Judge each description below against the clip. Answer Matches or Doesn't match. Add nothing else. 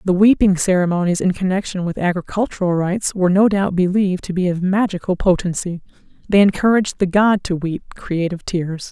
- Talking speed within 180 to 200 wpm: Doesn't match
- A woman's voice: Matches